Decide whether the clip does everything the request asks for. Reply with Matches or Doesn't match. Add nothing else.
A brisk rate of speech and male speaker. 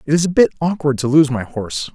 Matches